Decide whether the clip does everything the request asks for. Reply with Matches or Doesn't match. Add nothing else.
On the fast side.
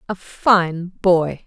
Doesn't match